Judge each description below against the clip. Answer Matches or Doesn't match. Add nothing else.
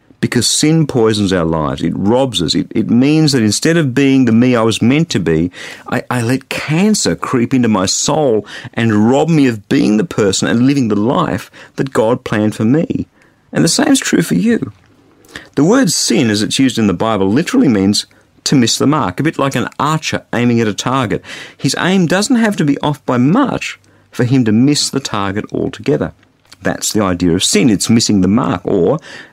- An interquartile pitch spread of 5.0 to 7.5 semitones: Matches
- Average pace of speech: Doesn't match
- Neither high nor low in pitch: Doesn't match